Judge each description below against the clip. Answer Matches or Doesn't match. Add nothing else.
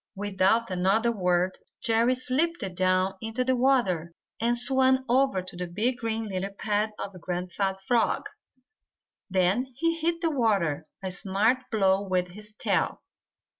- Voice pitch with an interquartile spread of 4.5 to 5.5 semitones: Matches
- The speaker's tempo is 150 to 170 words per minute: Doesn't match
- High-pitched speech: Matches